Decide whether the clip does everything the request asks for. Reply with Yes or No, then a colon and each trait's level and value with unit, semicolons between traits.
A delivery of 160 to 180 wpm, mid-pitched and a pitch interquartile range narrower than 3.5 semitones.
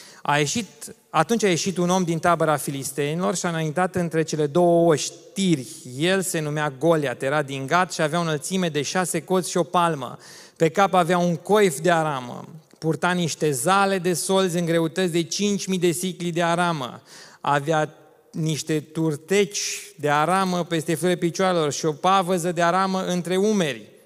Yes: fast, 170 wpm; medium, 170 Hz; average, 2.9 semitones